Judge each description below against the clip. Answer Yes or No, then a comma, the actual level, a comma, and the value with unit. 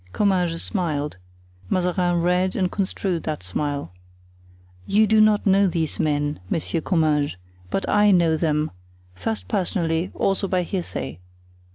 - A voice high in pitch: No, medium, 175 Hz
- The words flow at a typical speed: No, slow, 130 wpm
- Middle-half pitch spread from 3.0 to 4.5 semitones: Yes, average, 4.1 semitones